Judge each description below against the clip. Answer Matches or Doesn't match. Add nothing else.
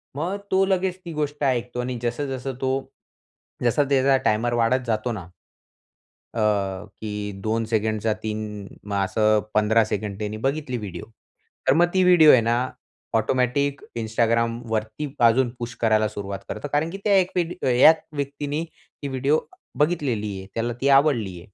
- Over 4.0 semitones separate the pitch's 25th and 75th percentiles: Matches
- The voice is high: Doesn't match